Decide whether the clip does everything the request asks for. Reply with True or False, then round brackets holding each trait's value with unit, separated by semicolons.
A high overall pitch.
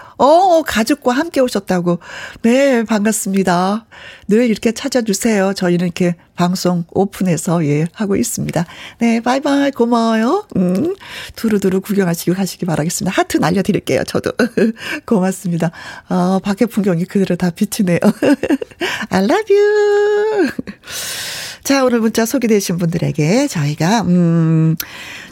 True (210 Hz)